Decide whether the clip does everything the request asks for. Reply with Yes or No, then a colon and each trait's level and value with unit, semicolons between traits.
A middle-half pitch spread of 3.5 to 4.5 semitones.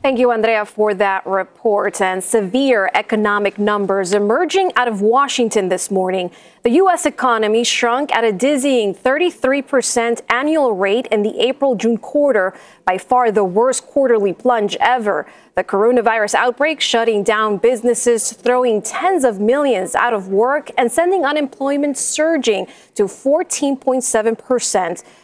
Yes: average, 4.2 semitones